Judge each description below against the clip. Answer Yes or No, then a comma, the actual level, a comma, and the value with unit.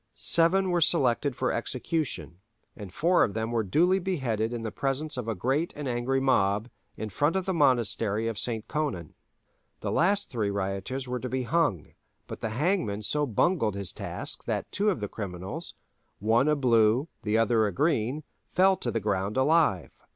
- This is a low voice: Yes, low, 120 Hz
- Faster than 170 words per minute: Yes, average, 180 wpm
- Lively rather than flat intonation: Yes, wide, 6.2 semitones